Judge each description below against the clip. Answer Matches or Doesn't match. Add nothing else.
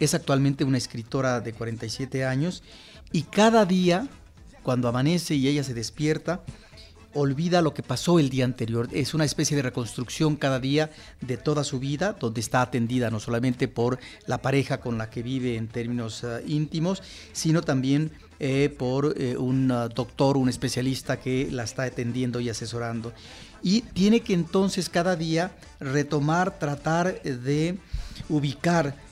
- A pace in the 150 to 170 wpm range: Matches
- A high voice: Doesn't match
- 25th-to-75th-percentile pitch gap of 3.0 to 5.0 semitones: Matches